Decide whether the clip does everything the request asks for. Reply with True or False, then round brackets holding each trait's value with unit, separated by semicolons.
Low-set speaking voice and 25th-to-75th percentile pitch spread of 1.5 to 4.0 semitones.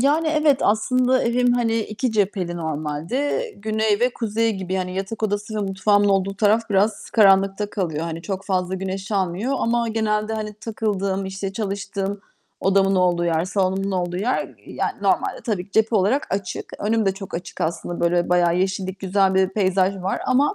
False (195 Hz; 2.8 semitones)